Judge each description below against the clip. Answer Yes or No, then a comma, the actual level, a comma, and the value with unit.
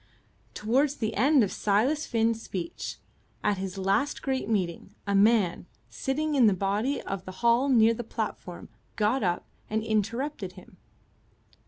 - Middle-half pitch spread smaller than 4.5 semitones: No, average, 4.8 semitones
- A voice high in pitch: Yes, high, 220 Hz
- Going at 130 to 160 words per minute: Yes, average, 150 wpm